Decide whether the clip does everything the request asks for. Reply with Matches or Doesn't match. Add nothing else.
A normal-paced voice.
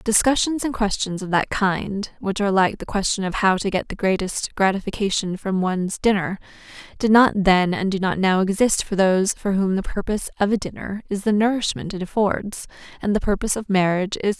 Doesn't match